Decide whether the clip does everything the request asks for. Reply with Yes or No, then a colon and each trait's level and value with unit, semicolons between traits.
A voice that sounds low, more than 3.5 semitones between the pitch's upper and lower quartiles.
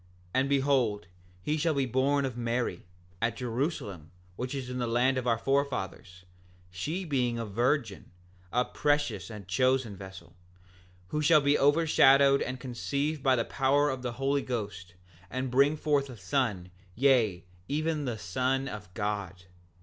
Yes: low, 130 Hz; average, 4.3 semitones